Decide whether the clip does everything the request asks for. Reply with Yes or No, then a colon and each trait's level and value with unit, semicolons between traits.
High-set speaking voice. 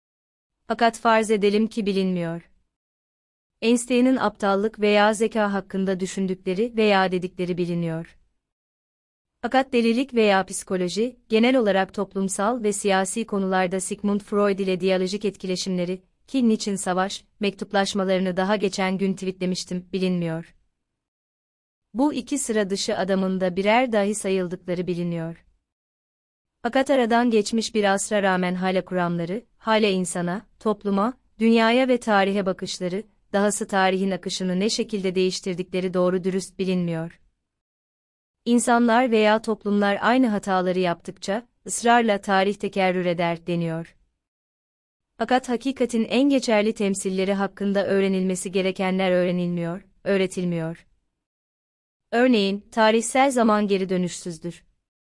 Yes: high, 195 Hz